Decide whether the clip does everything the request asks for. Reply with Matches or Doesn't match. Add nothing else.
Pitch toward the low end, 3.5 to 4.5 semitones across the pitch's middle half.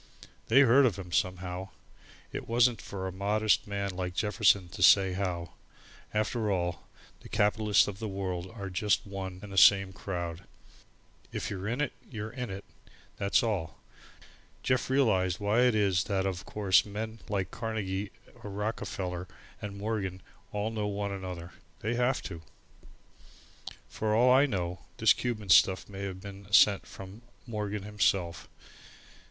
Doesn't match